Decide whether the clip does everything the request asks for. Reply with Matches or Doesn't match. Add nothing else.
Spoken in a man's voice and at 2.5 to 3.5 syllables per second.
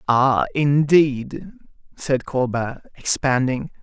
Matches